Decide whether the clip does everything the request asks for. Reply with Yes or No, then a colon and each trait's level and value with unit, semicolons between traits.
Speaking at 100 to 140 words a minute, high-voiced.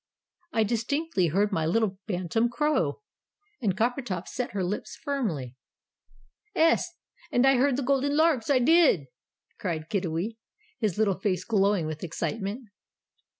Yes: slow, 135 wpm; high, 220 Hz